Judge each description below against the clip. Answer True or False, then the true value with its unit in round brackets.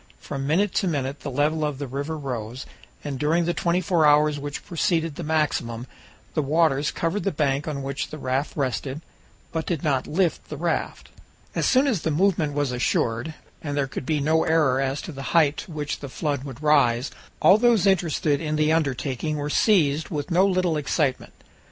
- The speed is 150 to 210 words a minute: True (195 wpm)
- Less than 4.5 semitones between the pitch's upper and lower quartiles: True (2.9 semitones)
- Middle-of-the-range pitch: True (150 Hz)